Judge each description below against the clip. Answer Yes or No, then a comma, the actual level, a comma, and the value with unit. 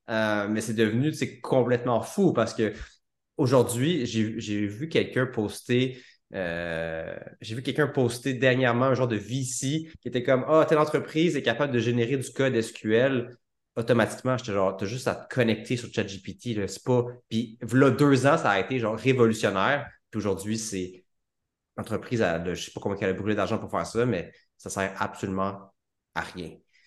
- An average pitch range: Yes, average, 4.0 semitones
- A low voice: Yes, low, 115 Hz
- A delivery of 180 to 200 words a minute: Yes, average, 190 wpm